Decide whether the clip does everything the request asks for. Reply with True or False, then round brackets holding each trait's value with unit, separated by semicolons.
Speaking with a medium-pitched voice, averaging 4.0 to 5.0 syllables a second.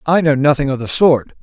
False (145 Hz; 5.6 syllables/s)